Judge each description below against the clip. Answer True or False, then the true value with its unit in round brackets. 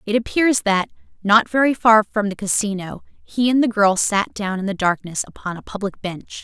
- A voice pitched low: False (210 Hz)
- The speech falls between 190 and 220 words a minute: True (205 wpm)